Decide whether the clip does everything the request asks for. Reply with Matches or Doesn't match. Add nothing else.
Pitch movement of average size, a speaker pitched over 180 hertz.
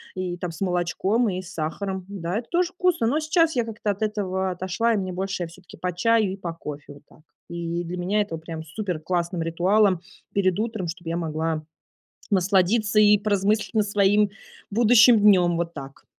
Matches